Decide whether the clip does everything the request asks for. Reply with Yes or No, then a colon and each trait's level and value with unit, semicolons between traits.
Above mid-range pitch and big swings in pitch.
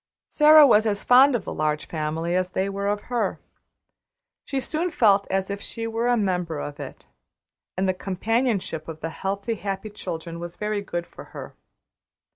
No: high, 200 Hz; average, 4.7 semitones